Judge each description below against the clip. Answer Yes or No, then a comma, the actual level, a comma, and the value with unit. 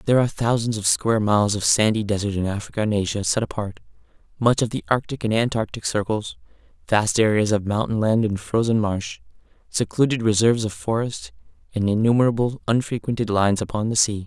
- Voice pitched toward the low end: Yes, low, 110 Hz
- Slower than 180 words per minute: Yes, average, 170 wpm